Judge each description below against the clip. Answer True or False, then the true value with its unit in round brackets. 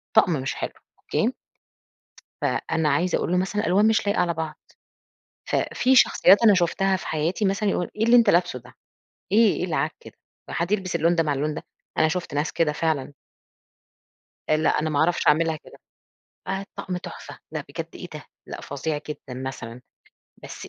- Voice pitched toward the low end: False (170 Hz)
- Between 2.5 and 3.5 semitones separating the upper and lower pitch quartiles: False (4.2 semitones)